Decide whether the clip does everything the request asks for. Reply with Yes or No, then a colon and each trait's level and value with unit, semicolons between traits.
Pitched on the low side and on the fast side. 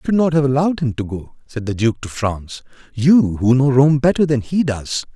Yes: low, 130 Hz; fast, 245 wpm